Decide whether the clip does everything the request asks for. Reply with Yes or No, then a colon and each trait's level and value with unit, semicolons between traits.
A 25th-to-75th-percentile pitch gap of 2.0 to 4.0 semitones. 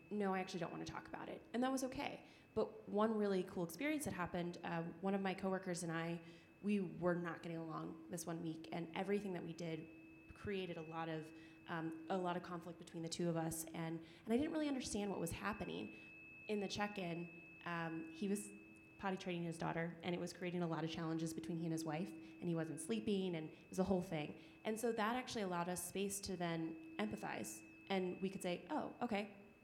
Yes: average, 2.9 semitones